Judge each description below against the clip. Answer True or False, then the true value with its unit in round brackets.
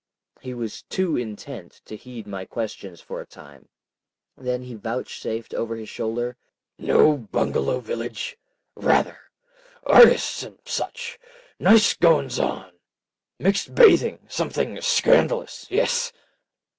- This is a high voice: False (125 Hz)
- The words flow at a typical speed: False (105 wpm)